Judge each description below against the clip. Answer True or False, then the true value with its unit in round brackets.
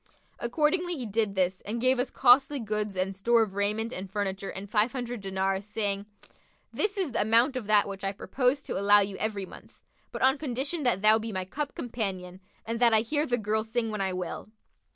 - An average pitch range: True (4.0 semitones)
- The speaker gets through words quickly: True (215 wpm)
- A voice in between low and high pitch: False (220 Hz)